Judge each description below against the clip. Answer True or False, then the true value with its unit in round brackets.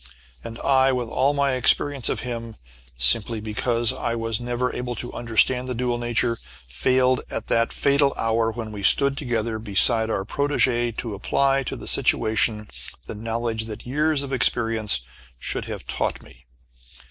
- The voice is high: False (120 Hz)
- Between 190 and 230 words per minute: False (160 wpm)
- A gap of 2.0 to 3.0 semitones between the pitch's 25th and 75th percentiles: True (2.4 semitones)